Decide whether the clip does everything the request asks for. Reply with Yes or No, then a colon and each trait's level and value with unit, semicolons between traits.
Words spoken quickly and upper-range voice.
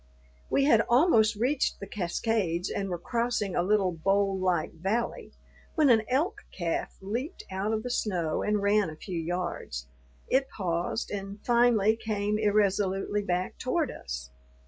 No: average, 150 wpm; high, 205 Hz